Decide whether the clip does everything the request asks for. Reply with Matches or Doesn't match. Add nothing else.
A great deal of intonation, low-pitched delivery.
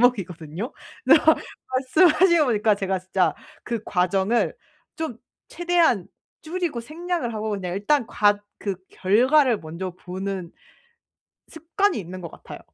Doesn't match